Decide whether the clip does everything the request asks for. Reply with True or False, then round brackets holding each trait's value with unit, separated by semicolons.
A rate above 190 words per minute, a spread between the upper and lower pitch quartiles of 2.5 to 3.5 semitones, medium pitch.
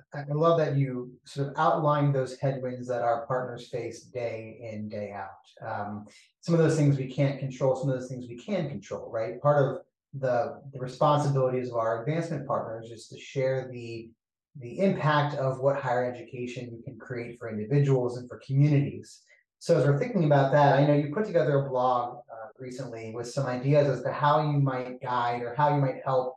False (205 wpm; 3.2 semitones; 130 Hz)